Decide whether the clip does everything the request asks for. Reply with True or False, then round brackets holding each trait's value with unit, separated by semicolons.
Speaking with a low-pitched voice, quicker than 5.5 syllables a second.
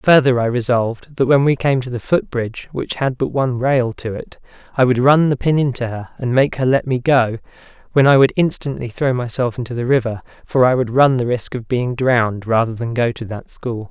False (125 Hz; 5.4 syllables/s)